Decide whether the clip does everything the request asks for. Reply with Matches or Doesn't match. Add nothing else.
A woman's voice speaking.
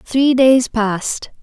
Matches